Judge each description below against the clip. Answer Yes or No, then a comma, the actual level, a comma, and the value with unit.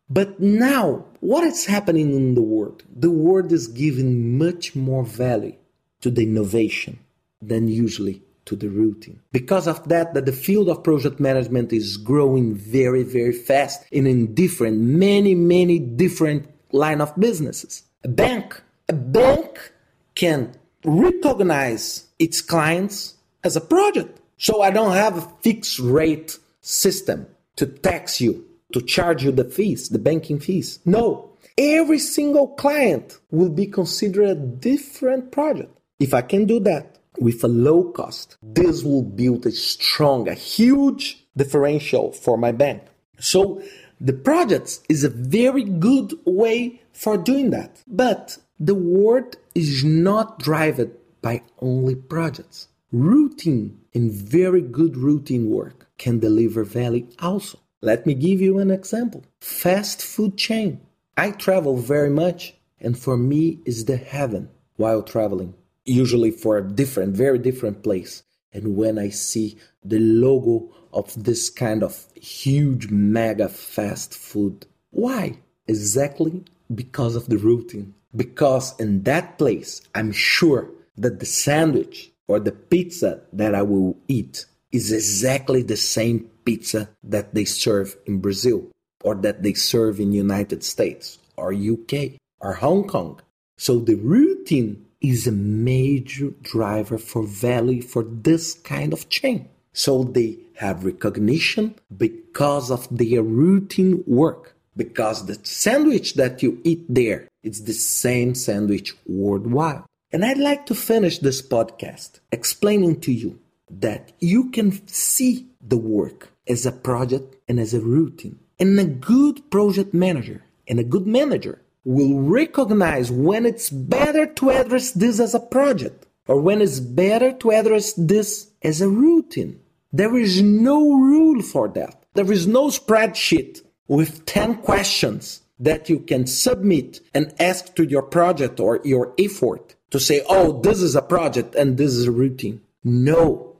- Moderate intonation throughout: No, wide, 8.6 semitones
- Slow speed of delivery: No, average, 145 wpm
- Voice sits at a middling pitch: Yes, medium, 150 Hz